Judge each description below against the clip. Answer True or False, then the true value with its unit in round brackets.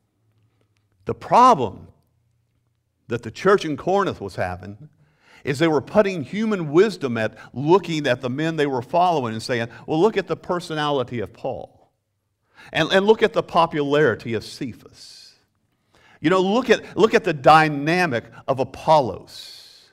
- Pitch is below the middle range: False (145 Hz)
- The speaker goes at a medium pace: True (150 wpm)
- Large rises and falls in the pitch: True (7.3 semitones)